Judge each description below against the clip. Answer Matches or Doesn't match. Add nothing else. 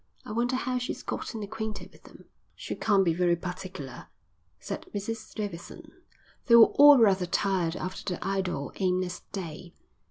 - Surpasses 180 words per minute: Doesn't match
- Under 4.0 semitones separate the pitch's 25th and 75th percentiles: Matches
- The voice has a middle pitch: Doesn't match